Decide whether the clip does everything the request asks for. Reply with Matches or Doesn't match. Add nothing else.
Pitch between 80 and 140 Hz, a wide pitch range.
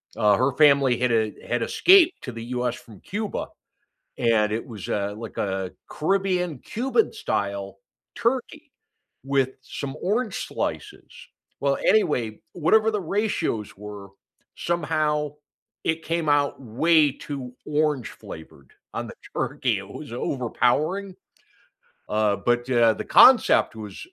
Matches